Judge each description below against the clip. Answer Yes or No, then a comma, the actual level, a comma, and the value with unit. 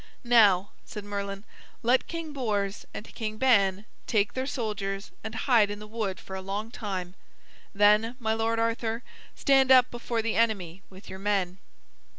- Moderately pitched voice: No, high, 215 Hz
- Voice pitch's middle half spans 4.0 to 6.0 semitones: No, average, 2.7 semitones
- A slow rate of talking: No, average, 165 wpm